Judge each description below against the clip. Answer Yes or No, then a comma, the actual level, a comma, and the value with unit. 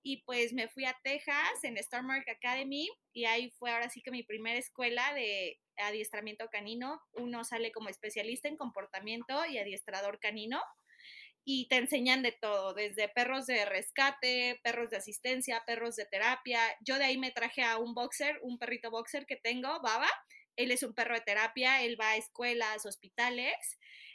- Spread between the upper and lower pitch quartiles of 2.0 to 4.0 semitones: Yes, average, 2.8 semitones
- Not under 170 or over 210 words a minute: Yes, average, 175 wpm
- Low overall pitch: No, high, 240 Hz